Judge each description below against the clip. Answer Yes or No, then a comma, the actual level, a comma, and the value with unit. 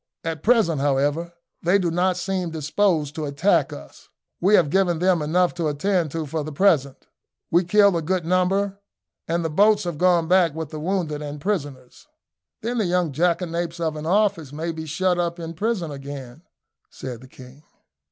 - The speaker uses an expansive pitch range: No, average, 3.5 semitones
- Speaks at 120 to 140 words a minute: No, average, 180 wpm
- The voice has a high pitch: No, medium, 170 Hz